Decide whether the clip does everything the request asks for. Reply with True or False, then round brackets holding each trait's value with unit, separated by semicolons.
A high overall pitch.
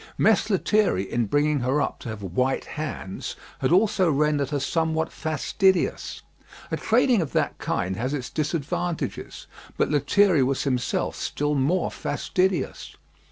False (150 Hz)